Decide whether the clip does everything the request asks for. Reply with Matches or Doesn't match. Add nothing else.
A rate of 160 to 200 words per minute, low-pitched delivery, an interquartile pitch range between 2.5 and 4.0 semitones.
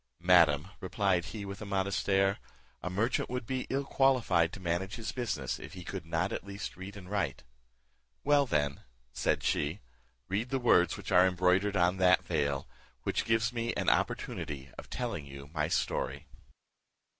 Doesn't match